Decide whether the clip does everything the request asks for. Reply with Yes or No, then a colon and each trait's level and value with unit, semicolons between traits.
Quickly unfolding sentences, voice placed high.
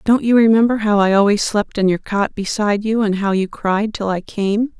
Yes: fast, 240 wpm; high, 210 Hz